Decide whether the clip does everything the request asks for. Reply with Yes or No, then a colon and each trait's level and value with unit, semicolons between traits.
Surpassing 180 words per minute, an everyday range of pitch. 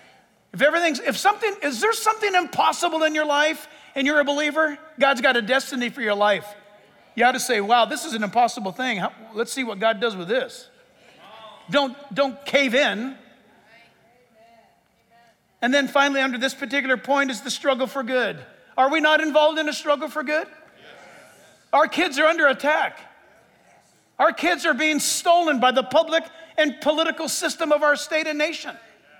No: average, 175 wpm; average, 3.8 semitones